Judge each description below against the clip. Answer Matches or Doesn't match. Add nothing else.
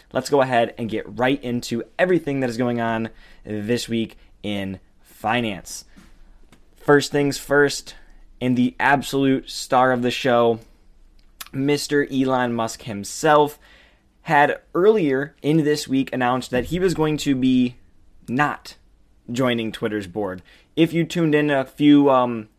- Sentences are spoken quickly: Doesn't match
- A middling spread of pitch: Matches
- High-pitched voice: Doesn't match